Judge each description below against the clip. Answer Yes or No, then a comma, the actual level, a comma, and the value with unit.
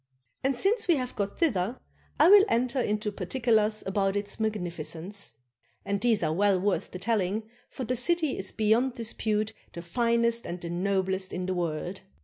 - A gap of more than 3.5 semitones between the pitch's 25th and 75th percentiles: Yes, average, 4.1 semitones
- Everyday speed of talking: Yes, average, 175 wpm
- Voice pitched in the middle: No, high, 210 Hz